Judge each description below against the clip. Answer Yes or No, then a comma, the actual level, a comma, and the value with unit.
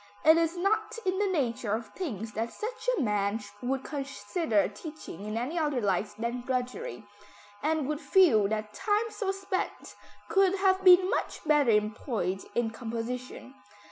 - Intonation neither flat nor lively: No, wide, 8.8 semitones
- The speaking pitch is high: Yes, very high, 260 Hz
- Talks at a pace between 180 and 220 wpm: No, average, 155 wpm